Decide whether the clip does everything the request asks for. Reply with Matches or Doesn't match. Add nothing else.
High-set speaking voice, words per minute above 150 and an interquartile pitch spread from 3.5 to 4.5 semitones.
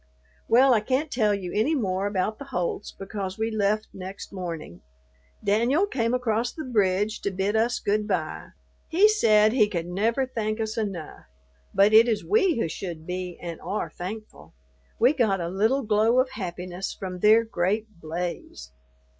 Matches